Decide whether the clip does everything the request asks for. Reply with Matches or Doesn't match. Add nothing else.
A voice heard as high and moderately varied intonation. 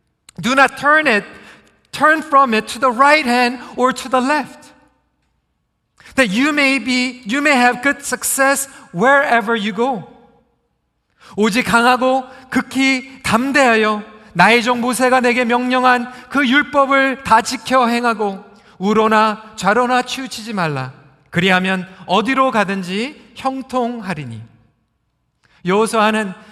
Matches